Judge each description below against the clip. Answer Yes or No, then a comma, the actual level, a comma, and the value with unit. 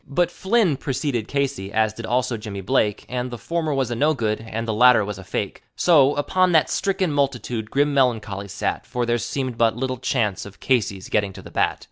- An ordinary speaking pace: No, fast, 210 wpm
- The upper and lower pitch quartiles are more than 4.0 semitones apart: Yes, average, 4.4 semitones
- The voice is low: Yes, low, 125 Hz